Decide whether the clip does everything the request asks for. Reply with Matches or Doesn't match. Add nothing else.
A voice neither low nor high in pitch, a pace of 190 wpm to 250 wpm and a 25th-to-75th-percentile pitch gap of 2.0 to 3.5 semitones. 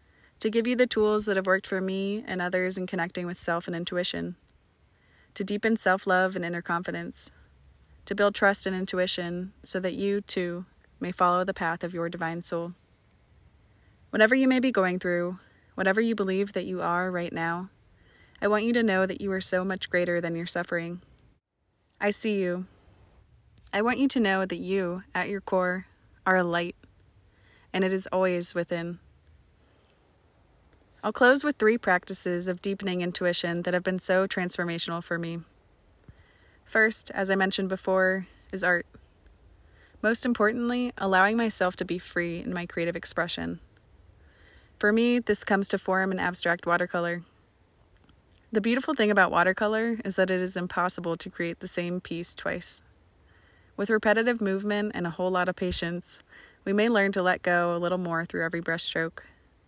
Doesn't match